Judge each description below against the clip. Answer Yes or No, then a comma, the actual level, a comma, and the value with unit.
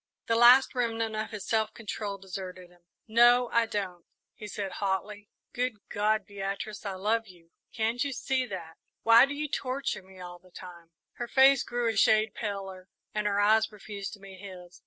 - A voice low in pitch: No, high, 210 Hz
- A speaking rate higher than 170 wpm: Yes, average, 185 wpm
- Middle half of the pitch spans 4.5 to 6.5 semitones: No, average, 3.3 semitones